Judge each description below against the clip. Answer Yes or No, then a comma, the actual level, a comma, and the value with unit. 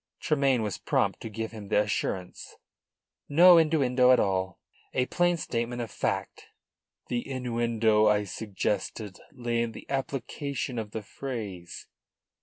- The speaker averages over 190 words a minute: No, slow, 135 wpm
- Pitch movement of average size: Yes, average, 4.0 semitones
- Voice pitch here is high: No, low, 115 Hz